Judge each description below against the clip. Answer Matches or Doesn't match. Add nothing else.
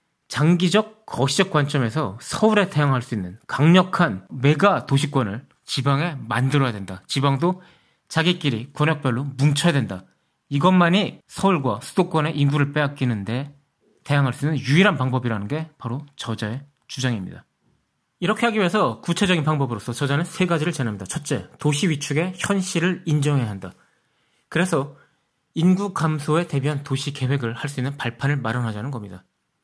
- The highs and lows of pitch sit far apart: Doesn't match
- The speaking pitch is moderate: Matches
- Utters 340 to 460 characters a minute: Matches